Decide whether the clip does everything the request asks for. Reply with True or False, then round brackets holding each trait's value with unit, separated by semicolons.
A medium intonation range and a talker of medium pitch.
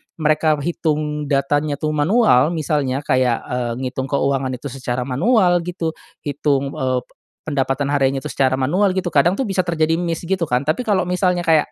True (4.3 semitones; 150 Hz)